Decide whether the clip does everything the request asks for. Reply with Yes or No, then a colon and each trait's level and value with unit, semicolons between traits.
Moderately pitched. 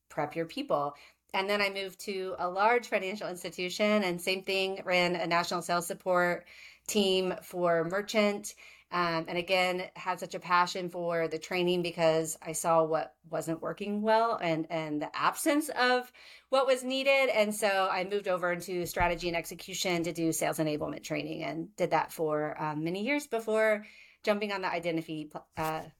Yes: medium, 180 Hz